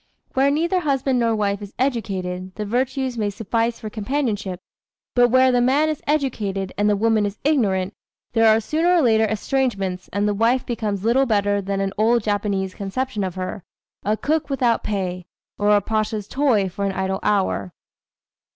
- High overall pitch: Yes, high, 215 Hz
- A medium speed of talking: Yes, average, 175 wpm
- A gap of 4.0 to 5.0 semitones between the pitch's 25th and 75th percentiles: Yes, average, 4.4 semitones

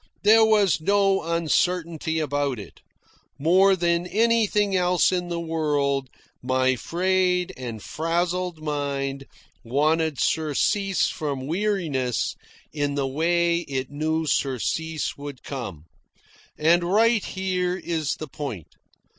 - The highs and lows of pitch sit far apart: No, average, 4.3 semitones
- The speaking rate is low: Yes, slow, 115 wpm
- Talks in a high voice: No, medium, 160 Hz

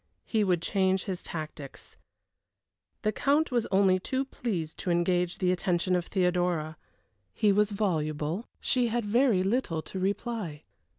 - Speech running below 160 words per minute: Yes, average, 140 wpm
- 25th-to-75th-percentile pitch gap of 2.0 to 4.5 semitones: Yes, average, 3.8 semitones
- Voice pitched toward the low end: No, medium, 185 Hz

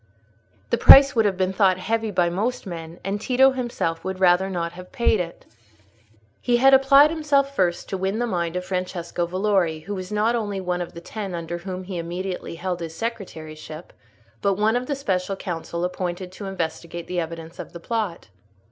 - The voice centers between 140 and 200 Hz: Yes, medium, 185 Hz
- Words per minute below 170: No, average, 190 wpm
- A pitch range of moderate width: Yes, average, 4.0 semitones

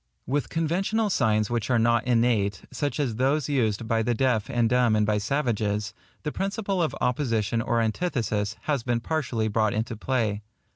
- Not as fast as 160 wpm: No, average, 175 wpm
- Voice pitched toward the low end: Yes, low, 120 Hz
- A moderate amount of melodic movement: Yes, average, 4.4 semitones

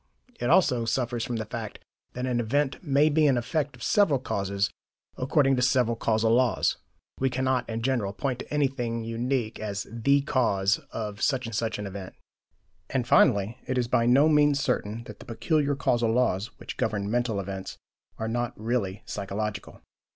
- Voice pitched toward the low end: Yes, low, 120 Hz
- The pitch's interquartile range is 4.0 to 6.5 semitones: No, average, 3.4 semitones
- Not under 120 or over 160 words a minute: No, average, 175 wpm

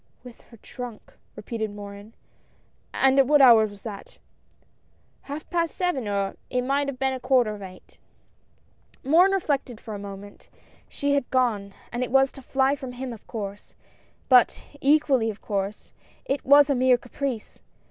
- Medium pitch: No, very high, 250 Hz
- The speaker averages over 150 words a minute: Yes, average, 190 wpm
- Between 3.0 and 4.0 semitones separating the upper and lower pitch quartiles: No, average, 4.5 semitones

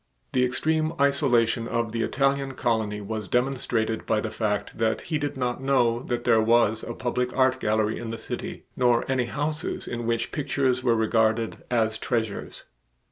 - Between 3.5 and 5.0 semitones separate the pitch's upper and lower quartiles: No, average, 2.8 semitones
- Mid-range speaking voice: No, low, 120 Hz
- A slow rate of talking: No, average, 170 wpm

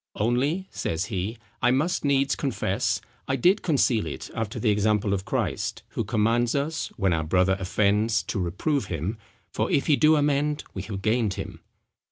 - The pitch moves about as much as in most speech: No, wide, 6.0 semitones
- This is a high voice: No, low, 115 Hz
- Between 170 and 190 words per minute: Yes, average, 175 wpm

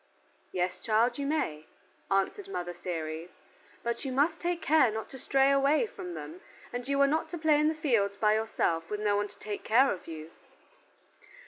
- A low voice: No, high, 225 Hz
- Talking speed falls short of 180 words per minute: No, average, 195 wpm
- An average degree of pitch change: No, wide, 7.4 semitones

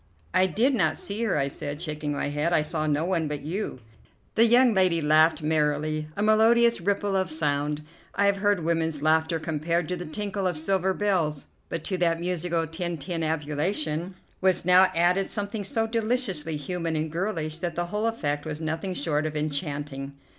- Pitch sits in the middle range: Yes, medium, 165 Hz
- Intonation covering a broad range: No, average, 3.9 semitones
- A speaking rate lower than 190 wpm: Yes, average, 180 wpm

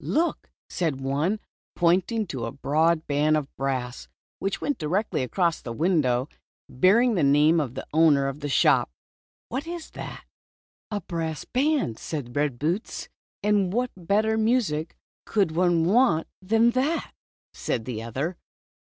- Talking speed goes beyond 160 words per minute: No, average, 155 wpm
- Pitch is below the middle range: No, medium, 165 Hz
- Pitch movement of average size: No, wide, 6.9 semitones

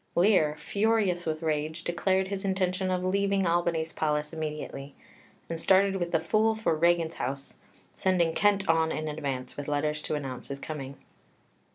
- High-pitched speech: No, medium, 165 Hz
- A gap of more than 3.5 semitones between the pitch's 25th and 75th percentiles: Yes, average, 3.9 semitones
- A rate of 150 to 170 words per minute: Yes, average, 160 wpm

